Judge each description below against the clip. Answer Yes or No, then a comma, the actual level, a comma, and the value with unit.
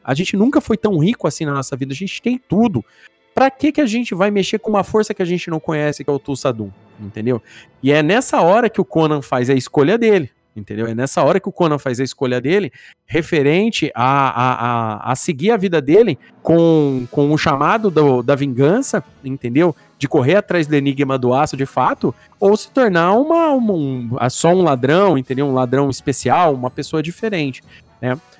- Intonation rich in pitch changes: Yes, wide, 6.9 semitones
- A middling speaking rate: No, fast, 210 wpm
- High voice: No, medium, 150 Hz